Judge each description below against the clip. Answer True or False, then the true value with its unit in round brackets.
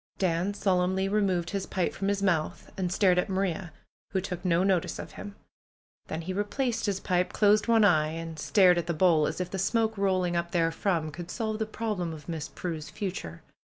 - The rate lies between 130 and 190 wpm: False (200 wpm)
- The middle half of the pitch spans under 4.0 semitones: True (2.8 semitones)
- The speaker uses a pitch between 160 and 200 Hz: True (185 Hz)